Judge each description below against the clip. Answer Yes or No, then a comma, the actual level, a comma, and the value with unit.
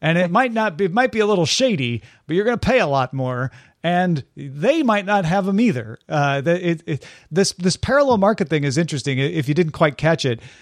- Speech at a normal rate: No, fast, 250 wpm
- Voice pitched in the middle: Yes, medium, 170 Hz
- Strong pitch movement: Yes, wide, 6.3 semitones